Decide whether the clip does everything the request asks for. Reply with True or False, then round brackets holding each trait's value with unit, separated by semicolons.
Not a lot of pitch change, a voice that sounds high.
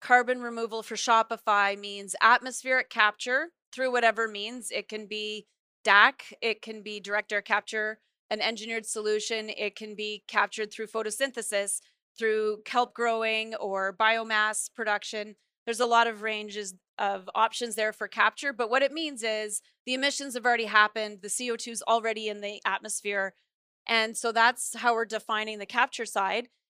True (1.8 semitones; 220 Hz)